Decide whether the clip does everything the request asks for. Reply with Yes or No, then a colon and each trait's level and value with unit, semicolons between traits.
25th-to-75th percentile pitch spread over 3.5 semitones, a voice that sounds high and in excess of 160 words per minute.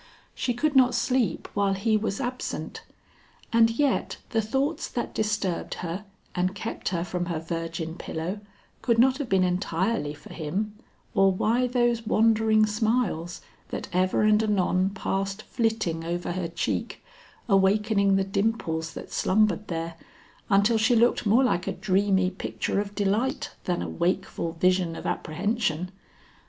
No: average, 3.9 semitones; high, 200 Hz; average, 145 wpm